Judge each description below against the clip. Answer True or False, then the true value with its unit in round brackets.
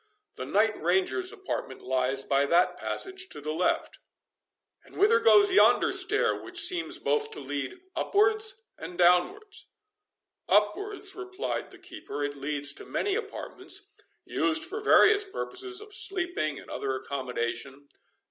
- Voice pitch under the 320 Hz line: False (365 Hz)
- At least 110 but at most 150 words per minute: True (140 wpm)